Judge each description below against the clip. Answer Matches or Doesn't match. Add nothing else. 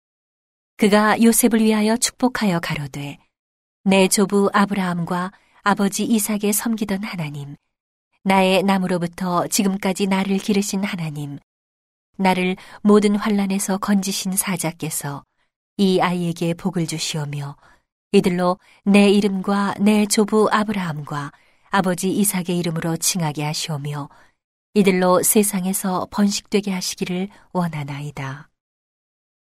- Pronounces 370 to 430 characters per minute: Doesn't match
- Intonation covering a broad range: Doesn't match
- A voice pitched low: Doesn't match